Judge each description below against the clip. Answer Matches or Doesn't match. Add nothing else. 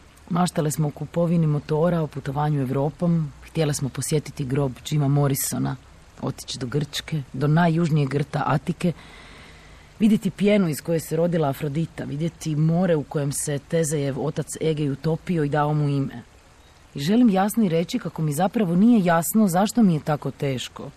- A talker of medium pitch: Matches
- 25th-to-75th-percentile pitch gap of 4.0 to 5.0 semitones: Doesn't match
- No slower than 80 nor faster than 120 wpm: Doesn't match